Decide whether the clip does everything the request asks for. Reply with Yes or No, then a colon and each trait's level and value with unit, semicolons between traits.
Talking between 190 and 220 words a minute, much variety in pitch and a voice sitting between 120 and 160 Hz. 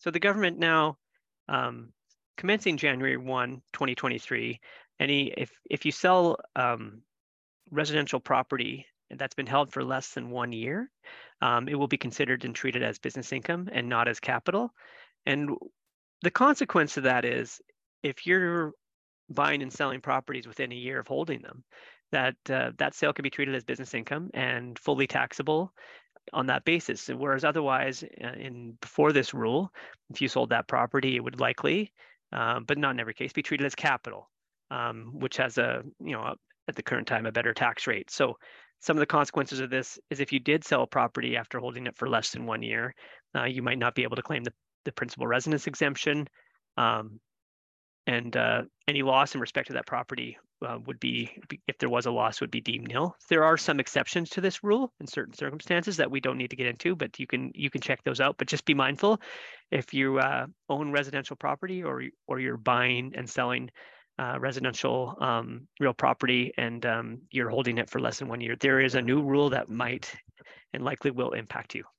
No: average, 200 wpm; average, 4.1 semitones; low, 135 Hz